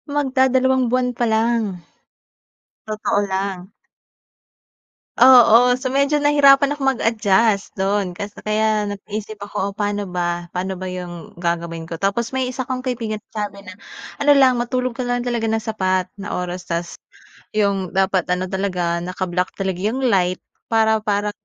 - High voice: Yes, high, 210 Hz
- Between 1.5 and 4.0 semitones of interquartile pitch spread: No, average, 4.8 semitones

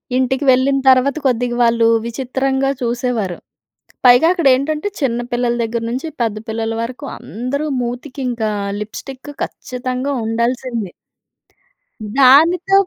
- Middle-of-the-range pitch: No, very high, 255 Hz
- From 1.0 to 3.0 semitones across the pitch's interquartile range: Yes, narrow, 2.5 semitones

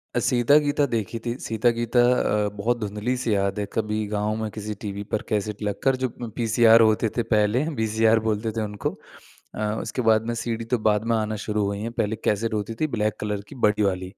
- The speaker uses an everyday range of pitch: No, narrow, 1.8 semitones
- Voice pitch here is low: Yes, low, 110 Hz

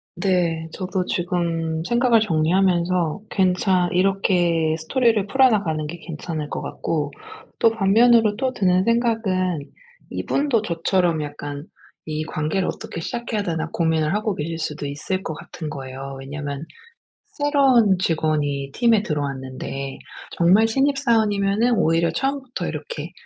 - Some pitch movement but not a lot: No, wide, 5.7 semitones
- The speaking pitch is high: No, medium, 180 Hz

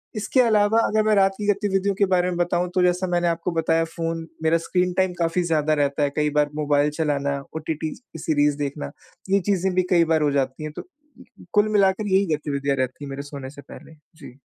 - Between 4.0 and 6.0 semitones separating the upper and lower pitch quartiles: Yes, average, 4.5 semitones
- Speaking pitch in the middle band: Yes, medium, 165 Hz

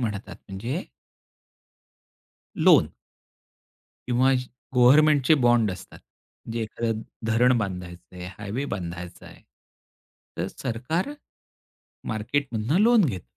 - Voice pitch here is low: Yes, low, 115 Hz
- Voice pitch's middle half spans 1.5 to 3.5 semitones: No, average, 4.8 semitones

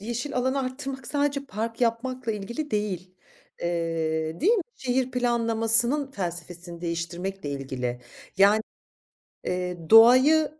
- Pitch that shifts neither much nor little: No, wide, 6.7 semitones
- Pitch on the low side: No, high, 225 Hz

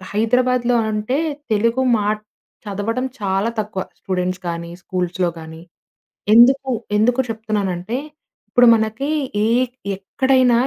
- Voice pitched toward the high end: Yes, high, 220 Hz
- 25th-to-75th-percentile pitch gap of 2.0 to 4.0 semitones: No, average, 4.6 semitones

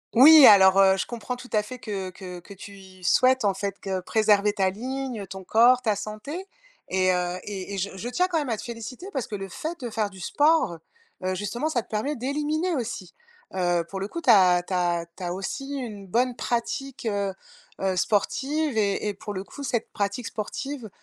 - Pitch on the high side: Yes, high, 210 Hz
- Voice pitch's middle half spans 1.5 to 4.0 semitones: No, average, 4.9 semitones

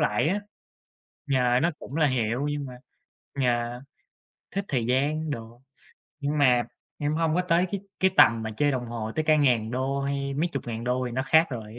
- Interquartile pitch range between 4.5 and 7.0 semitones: No, average, 3.8 semitones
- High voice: No, low, 130 Hz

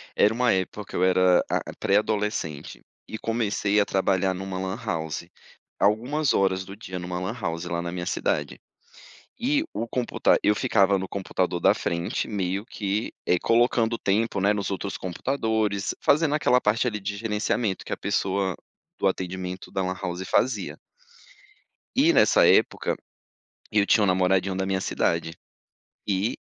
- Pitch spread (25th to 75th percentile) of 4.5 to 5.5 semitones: No, average, 3.1 semitones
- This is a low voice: Yes, low, 100 Hz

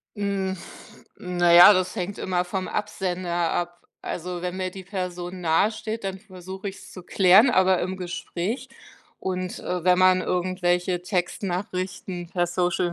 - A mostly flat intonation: Yes, narrow, 1.3 semitones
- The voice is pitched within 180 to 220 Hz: Yes, medium, 185 Hz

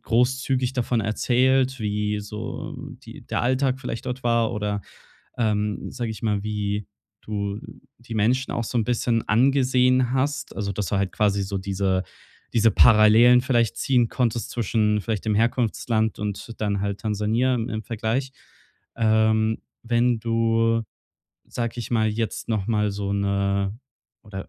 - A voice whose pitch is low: Yes, low, 110 Hz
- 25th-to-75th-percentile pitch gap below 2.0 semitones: No, narrow, 2.6 semitones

